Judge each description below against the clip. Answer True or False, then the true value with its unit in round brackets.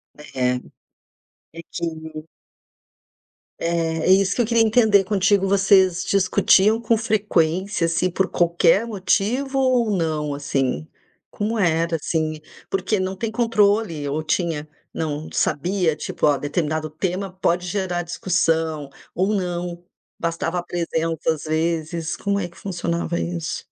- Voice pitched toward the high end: False (175 Hz)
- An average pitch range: True (3.7 semitones)